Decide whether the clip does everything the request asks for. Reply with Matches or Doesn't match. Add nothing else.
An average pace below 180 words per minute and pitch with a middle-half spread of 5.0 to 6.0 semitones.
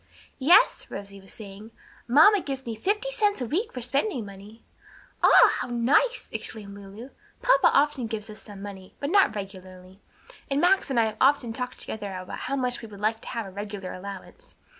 Doesn't match